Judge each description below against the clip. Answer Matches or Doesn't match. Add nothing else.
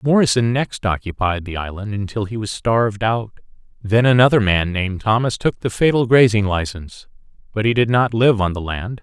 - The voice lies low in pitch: Matches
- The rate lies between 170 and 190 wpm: Matches